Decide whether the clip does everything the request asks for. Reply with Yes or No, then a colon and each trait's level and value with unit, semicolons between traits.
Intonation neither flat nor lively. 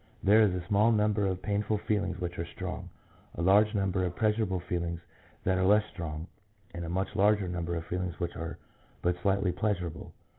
Yes: average, 3.1 semitones